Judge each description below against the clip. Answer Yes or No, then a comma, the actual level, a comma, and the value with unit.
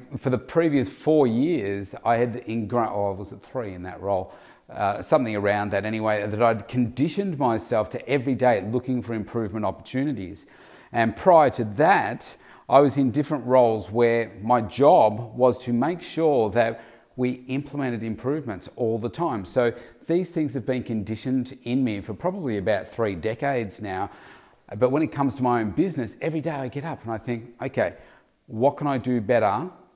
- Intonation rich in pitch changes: No, average, 3.5 semitones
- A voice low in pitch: Yes, low, 120 Hz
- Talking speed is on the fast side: No, average, 180 wpm